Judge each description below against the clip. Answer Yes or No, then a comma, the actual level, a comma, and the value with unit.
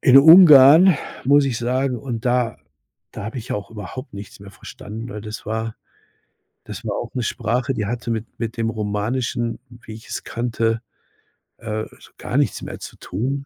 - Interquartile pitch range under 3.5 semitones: Yes, average, 2.9 semitones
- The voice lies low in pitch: Yes, low, 115 Hz